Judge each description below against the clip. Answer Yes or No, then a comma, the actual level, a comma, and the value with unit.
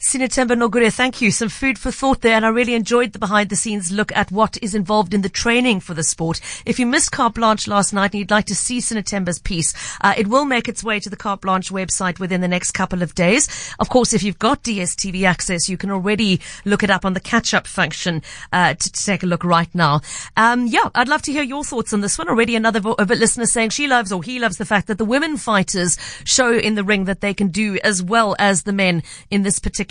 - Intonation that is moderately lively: Yes, average, 3.5 semitones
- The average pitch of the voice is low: No, high, 210 Hz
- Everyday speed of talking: No, fast, 260 wpm